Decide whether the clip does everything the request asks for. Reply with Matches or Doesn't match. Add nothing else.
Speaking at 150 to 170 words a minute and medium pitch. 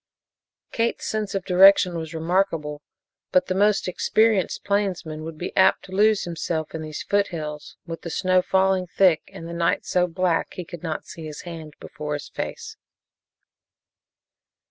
Matches